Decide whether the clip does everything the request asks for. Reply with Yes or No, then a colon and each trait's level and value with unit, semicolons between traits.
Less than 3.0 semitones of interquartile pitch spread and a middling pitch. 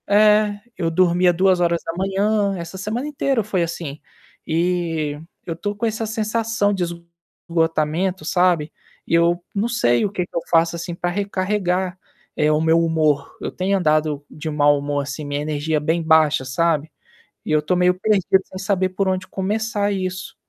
No: average, 3.8 semitones; medium, 175 Hz